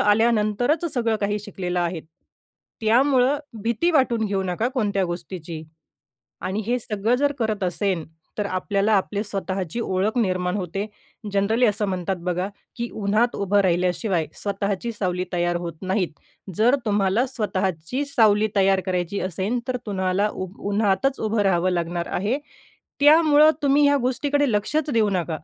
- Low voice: No, high, 205 Hz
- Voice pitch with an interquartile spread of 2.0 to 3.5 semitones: No, average, 4.1 semitones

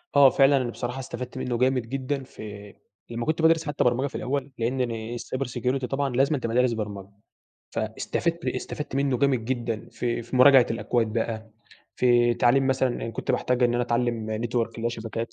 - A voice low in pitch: Yes, low, 125 Hz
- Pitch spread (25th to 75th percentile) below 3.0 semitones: Yes, narrow, 2.4 semitones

